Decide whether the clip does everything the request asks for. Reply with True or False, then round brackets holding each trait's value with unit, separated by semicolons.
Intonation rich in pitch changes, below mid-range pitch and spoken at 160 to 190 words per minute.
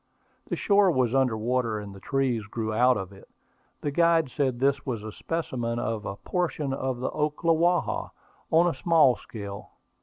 True (5.8 semitones; 130 Hz; 175 wpm)